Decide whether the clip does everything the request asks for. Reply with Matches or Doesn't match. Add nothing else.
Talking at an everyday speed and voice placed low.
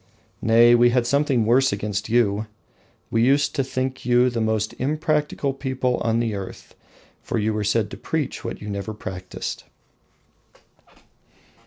Matches